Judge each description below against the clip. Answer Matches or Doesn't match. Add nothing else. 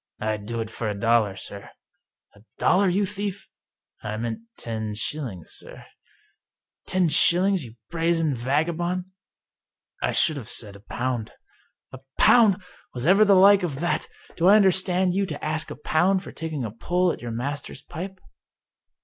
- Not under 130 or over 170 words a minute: Doesn't match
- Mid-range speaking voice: Matches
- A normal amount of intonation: Doesn't match